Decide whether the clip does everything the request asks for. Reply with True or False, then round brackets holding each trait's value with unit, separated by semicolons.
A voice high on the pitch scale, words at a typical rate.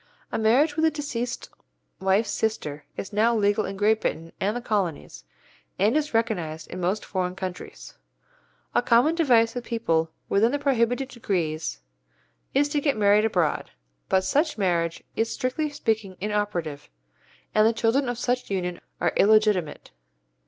True (215 Hz; 150 wpm)